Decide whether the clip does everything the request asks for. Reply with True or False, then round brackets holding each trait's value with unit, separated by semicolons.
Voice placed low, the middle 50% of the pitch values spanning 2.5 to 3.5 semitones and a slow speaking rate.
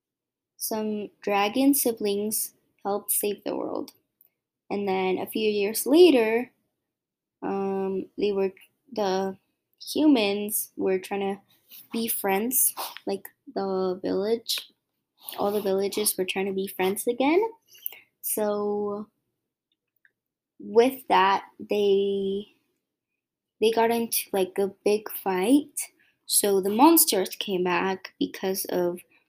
False (205 Hz; 3.1 semitones; 110 wpm)